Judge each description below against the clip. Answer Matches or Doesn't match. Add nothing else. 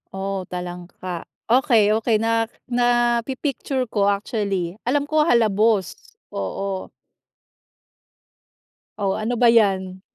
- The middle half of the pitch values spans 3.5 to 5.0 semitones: Matches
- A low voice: Doesn't match